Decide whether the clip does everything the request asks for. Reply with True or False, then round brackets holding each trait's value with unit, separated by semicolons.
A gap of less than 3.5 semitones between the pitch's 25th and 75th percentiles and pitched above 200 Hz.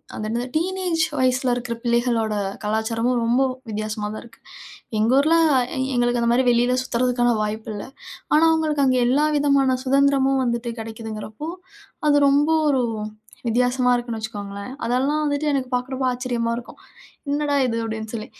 True (3.1 semitones; 245 Hz)